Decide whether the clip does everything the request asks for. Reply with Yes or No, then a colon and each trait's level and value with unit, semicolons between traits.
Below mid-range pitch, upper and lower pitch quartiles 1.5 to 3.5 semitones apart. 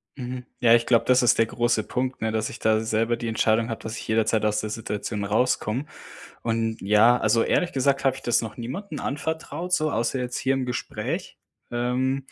Yes: low, 120 Hz; narrow, 2.6 semitones